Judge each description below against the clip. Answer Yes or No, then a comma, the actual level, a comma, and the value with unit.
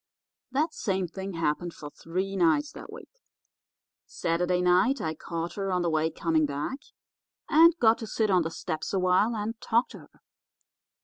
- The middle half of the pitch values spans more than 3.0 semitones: Yes, average, 5.1 semitones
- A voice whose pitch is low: No, medium, 185 Hz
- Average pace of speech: Yes, average, 175 wpm